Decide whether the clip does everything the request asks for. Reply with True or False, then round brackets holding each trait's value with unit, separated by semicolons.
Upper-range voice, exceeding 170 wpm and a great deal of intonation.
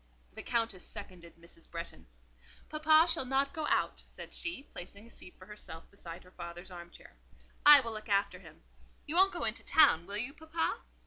True (210 Hz; 190 wpm; 9.0 semitones)